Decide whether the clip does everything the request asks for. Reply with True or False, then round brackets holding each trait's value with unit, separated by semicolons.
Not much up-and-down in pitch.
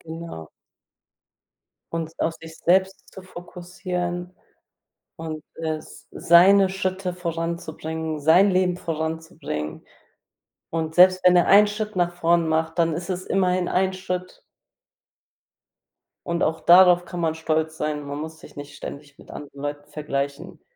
True (2.3 semitones)